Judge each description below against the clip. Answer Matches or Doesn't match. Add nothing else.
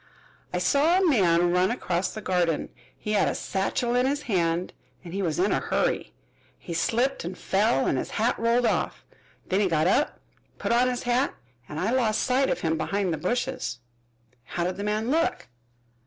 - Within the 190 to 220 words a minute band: Matches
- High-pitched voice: Matches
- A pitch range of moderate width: Doesn't match